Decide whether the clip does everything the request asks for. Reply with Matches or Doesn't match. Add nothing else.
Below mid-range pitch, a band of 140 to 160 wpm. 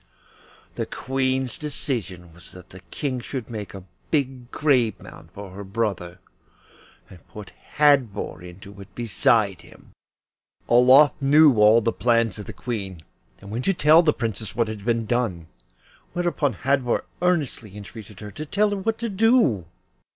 Matches